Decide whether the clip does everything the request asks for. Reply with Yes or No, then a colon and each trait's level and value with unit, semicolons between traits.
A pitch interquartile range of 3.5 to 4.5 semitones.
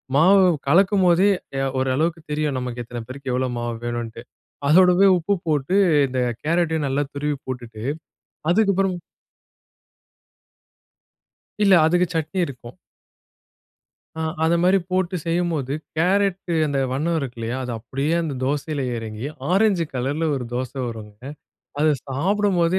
No: wide, 5.5 semitones